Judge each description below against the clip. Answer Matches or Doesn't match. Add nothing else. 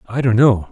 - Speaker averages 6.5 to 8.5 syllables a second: Doesn't match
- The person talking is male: Matches